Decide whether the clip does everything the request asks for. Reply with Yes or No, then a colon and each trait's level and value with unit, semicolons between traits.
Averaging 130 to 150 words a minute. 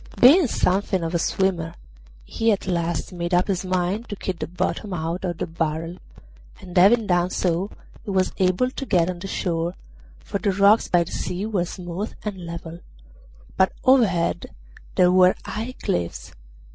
No: average, 170 wpm